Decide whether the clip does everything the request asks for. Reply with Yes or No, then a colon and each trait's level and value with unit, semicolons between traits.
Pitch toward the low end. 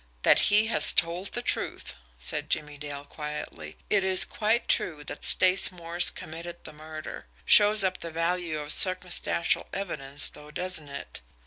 No: medium, 165 Hz